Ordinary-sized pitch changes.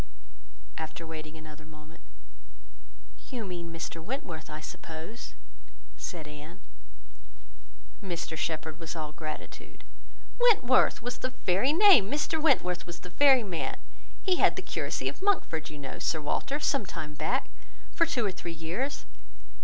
No: wide, 8.3 semitones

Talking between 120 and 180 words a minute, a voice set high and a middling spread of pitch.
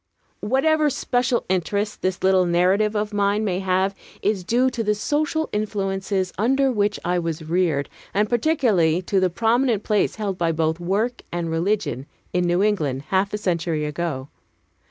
Yes: average, 160 wpm; high, 195 Hz; average, 3.7 semitones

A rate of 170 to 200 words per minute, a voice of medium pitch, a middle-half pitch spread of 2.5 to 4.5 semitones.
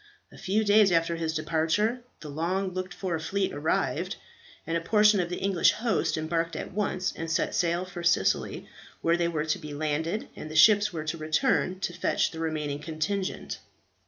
Yes: average, 190 wpm; medium, 170 Hz; average, 3.2 semitones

